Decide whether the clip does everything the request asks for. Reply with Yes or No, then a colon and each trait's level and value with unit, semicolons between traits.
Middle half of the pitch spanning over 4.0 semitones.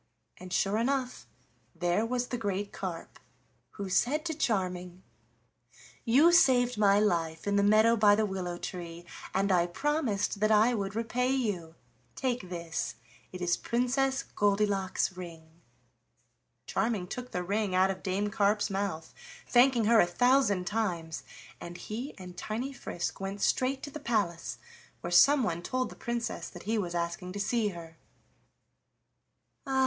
Yes: average, 5.0 semitones